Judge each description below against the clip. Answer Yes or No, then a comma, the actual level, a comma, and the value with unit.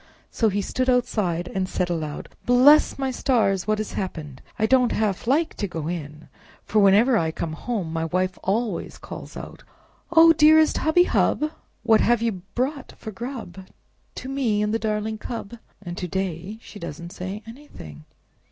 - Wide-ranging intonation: Yes, wide, 5.7 semitones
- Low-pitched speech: No, high, 210 Hz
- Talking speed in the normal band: Yes, average, 170 wpm